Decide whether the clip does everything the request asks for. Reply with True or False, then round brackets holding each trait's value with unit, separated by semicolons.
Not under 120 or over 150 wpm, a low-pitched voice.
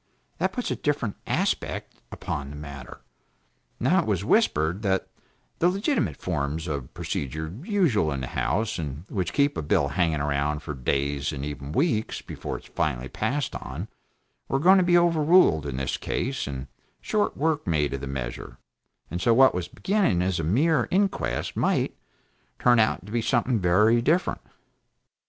False (170 wpm; 90 Hz)